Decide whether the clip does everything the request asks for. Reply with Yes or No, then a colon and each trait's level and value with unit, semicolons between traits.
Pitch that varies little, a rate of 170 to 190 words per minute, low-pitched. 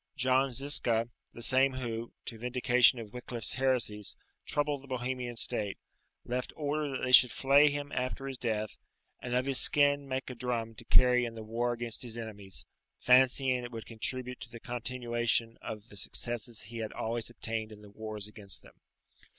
Yes: narrow, 2.3 semitones; average, 180 wpm; low, 120 Hz